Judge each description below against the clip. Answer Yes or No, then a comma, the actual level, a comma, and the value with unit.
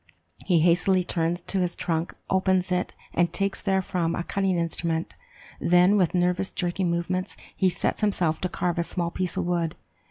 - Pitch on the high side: No, medium, 180 Hz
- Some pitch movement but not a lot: No, narrow, 1.6 semitones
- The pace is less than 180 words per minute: Yes, average, 170 wpm